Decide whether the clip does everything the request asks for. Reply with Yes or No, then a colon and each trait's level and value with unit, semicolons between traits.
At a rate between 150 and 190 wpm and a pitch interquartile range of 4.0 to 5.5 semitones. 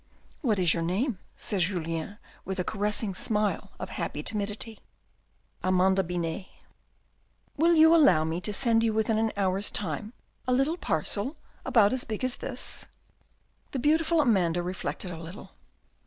Yes: average, 160 wpm; average, 4.8 semitones